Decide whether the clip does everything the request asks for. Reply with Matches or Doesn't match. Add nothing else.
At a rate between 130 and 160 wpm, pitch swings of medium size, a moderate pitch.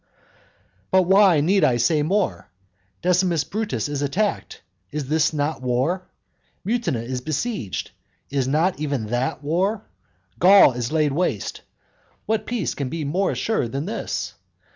Doesn't match